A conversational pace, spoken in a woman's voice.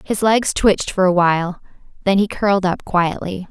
Yes: average, 190 wpm; female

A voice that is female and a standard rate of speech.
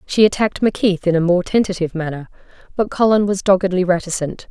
Yes: female; average, 175 wpm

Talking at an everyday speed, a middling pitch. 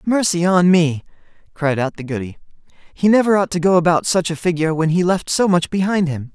No: fast, 215 wpm; medium, 170 Hz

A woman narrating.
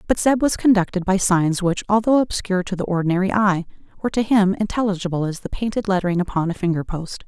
Yes: female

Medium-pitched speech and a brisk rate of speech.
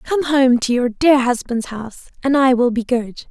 No: very high, 255 Hz; fast, 220 wpm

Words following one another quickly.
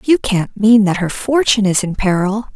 Yes: fast, 210 wpm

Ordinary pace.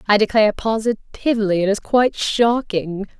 No: slow, 130 wpm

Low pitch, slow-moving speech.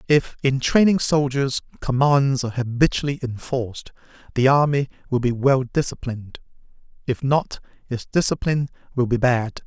Yes: low, 130 Hz; slow, 130 wpm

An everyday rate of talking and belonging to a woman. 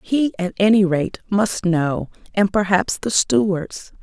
Yes: average, 150 wpm; female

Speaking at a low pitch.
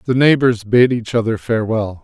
Yes: low, 115 Hz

